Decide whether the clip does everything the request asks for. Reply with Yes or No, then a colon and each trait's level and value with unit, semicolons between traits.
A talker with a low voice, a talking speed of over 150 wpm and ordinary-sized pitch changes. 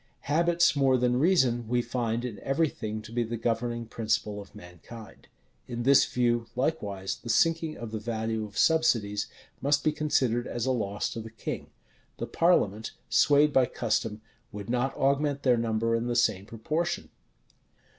Yes: low, 120 Hz; average, 165 wpm; average, 3.9 semitones